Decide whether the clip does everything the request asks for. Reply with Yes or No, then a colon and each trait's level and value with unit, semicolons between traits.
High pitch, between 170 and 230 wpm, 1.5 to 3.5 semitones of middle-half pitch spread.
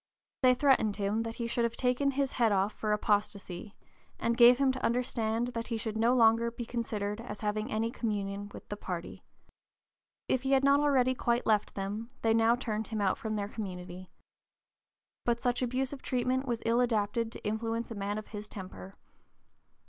Yes: high, 225 Hz; average, 185 wpm; average, 2.8 semitones